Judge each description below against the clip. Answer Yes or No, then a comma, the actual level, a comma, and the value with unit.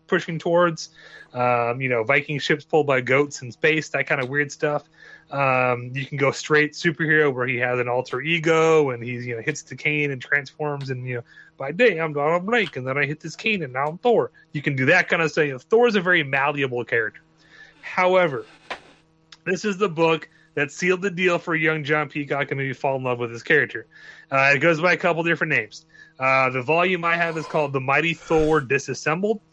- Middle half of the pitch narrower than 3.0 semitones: No, average, 3.7 semitones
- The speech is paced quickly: Yes, fast, 225 wpm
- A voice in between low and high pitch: Yes, medium, 150 Hz